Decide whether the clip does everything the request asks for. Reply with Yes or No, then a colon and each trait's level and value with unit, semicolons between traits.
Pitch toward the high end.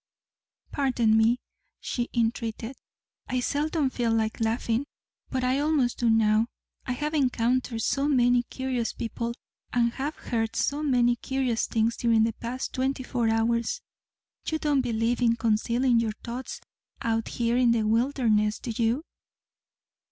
Yes: high, 240 Hz